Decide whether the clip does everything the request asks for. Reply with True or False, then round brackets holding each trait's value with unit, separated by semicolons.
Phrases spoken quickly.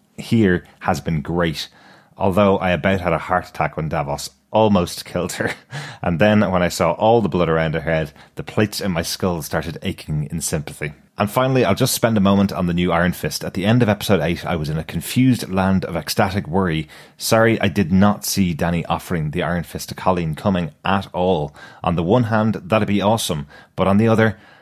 True (215 wpm)